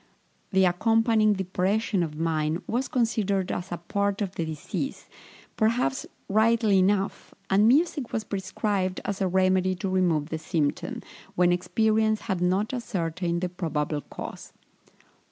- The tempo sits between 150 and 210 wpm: No, slow, 135 wpm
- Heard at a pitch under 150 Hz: No, high, 190 Hz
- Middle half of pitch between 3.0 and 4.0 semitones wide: Yes, average, 3.6 semitones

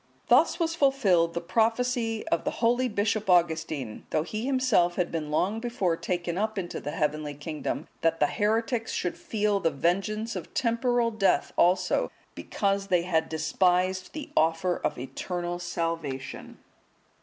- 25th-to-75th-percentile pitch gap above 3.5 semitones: Yes, average, 5.2 semitones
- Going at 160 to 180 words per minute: No, average, 150 wpm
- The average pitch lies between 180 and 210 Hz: Yes, medium, 185 Hz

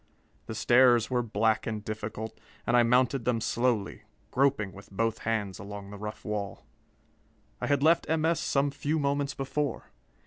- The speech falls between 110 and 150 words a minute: No, average, 165 wpm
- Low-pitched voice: Yes, low, 120 Hz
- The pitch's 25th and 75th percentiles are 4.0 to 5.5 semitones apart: Yes, average, 4.5 semitones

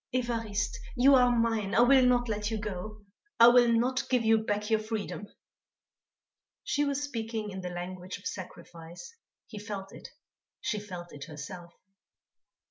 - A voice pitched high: Yes, high, 215 Hz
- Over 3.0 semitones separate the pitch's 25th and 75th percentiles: Yes, average, 3.9 semitones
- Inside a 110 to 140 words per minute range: No, average, 155 wpm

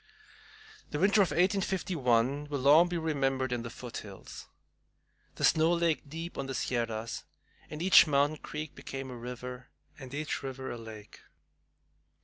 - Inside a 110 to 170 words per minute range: Yes, average, 145 wpm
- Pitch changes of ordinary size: Yes, average, 4.3 semitones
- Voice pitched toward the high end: No, medium, 140 Hz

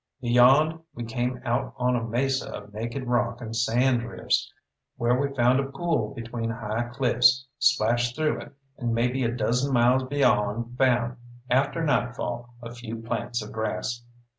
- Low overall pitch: Yes, low, 120 Hz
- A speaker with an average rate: Yes, average, 160 wpm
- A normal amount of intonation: No, narrow, 2.1 semitones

